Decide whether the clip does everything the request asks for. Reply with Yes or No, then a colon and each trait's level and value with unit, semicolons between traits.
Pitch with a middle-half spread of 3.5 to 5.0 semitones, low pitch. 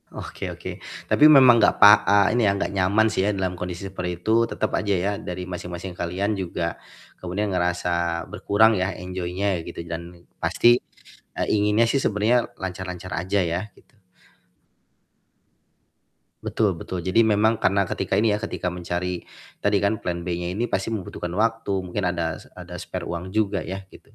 No: average, 2.9 semitones; very low, 95 Hz